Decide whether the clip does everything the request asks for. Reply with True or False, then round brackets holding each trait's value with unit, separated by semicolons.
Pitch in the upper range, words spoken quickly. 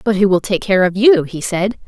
True (200 Hz; 290 wpm)